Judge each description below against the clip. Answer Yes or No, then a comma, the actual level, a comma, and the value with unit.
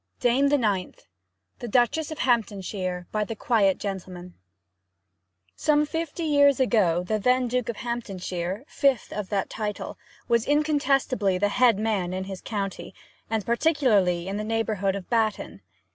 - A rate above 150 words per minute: No, average, 145 wpm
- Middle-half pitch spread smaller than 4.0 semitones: No, average, 4.7 semitones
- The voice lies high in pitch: Yes, high, 220 Hz